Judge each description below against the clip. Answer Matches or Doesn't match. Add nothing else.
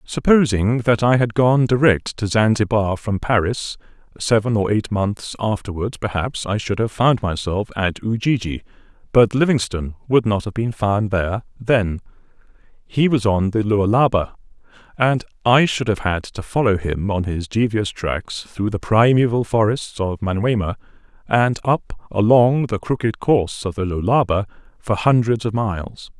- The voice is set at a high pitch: Doesn't match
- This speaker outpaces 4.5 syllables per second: Matches